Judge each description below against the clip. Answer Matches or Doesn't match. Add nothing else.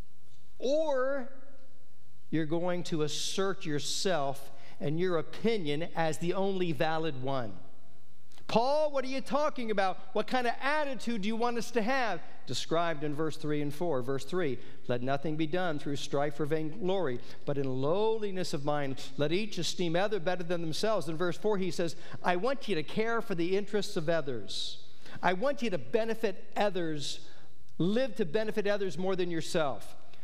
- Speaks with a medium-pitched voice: Matches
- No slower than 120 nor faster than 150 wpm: Doesn't match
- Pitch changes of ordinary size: Doesn't match